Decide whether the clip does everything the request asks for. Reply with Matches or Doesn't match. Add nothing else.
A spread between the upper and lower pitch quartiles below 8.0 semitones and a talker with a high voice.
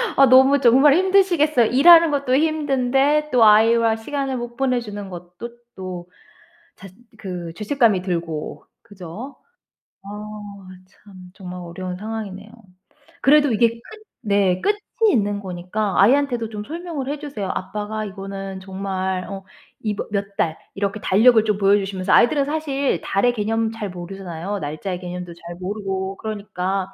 Matches